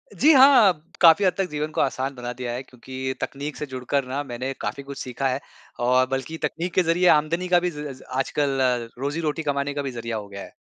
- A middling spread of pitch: Yes, average, 3.9 semitones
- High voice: No, medium, 140 Hz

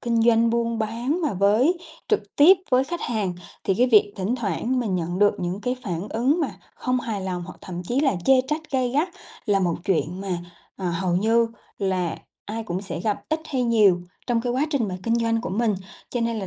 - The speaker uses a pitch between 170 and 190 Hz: No, high, 225 Hz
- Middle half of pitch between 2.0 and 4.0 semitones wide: No, average, 4.7 semitones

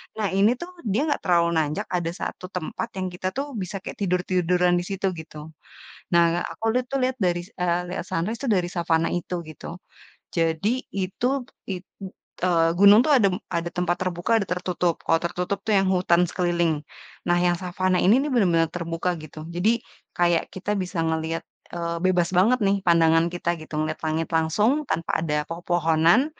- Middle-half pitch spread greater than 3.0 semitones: No, average, 2.7 semitones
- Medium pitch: Yes, medium, 180 Hz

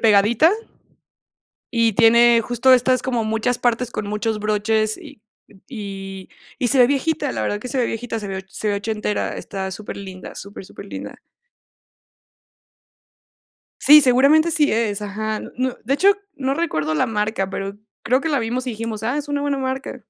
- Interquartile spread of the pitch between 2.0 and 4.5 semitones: Yes, average, 3.8 semitones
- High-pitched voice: Yes, high, 225 Hz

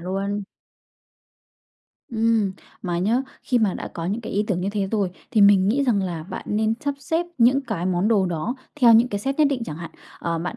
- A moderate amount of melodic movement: Yes, average, 4.0 semitones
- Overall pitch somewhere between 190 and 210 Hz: Yes, high, 205 Hz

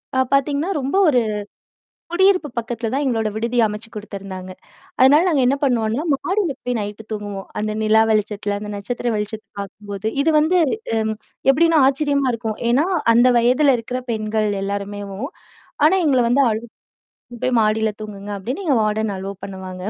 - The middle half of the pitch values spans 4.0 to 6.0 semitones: Yes, average, 4.5 semitones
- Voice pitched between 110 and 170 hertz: No, high, 225 Hz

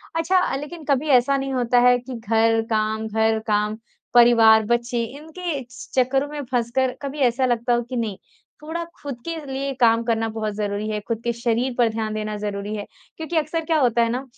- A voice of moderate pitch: No, high, 240 Hz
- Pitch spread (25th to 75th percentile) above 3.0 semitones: Yes, average, 3.6 semitones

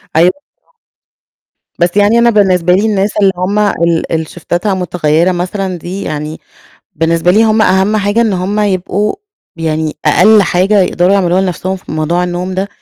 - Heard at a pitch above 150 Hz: Yes, medium, 185 Hz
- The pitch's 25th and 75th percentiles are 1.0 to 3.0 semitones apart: Yes, average, 2.7 semitones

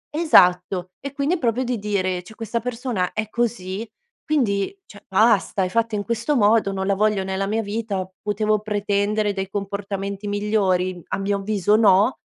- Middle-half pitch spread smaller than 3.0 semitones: Yes, narrow, 2.6 semitones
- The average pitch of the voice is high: Yes, high, 205 Hz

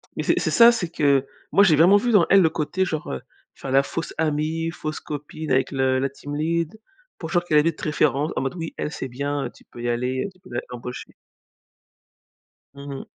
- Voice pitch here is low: No, medium, 150 Hz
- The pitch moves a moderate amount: Yes, average, 3.5 semitones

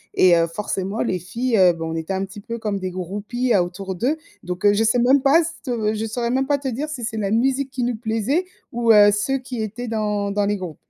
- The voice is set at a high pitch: Yes, high, 220 Hz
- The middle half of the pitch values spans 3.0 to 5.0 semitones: Yes, average, 4.1 semitones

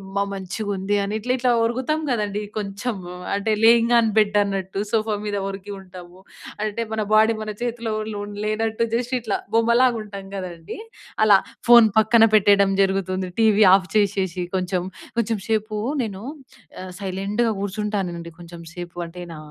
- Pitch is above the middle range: Yes, high, 205 Hz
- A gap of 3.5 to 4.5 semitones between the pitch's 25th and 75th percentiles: No, average, 2.8 semitones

